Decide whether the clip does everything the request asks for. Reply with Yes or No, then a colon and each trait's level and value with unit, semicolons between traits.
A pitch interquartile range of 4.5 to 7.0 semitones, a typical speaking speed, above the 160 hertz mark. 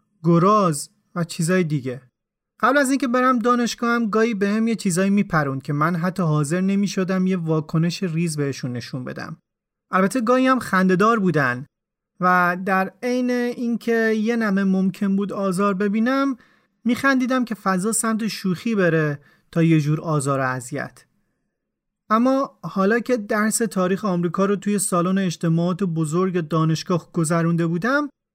Yes: average, 4.9 semitones; average, 145 wpm; high, 190 Hz